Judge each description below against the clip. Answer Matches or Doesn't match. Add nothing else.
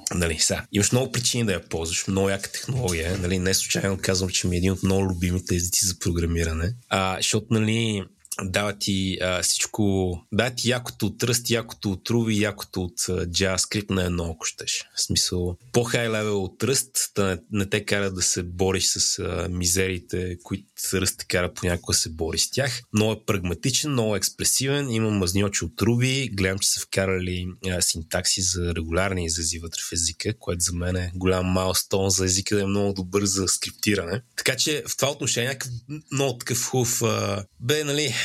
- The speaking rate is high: Matches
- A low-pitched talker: Matches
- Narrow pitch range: Doesn't match